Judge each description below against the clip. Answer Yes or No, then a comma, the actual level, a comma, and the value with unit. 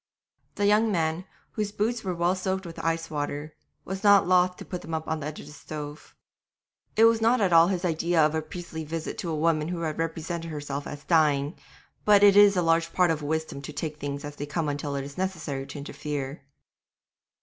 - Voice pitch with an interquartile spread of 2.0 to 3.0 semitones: No, average, 3.5 semitones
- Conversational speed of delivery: No, fast, 220 wpm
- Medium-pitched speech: Yes, medium, 165 Hz